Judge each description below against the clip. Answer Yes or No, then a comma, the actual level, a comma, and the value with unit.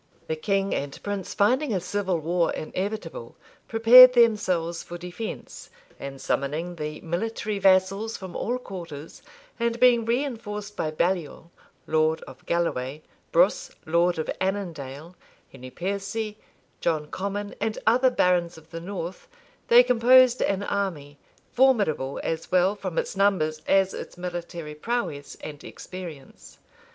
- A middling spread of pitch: Yes, average, 4.8 semitones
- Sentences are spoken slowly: Yes, slow, 130 wpm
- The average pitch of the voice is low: No, medium, 185 Hz